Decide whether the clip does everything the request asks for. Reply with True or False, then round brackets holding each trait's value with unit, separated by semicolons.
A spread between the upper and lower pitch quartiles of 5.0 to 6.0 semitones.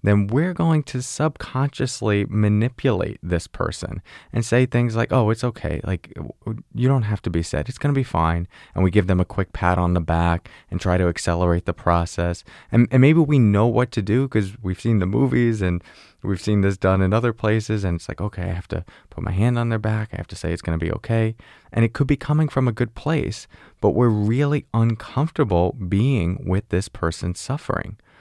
True (5.5 semitones)